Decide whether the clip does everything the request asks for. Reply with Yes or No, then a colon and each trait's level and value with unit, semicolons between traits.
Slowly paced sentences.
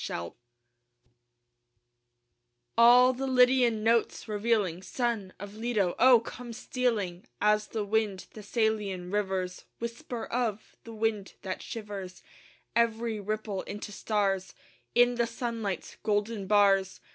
Yes: slow, 115 wpm